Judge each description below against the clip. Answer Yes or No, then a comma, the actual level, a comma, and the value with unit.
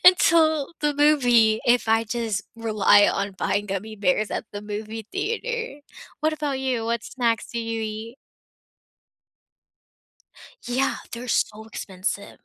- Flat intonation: No, average, 4.4 semitones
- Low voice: No, high, 230 Hz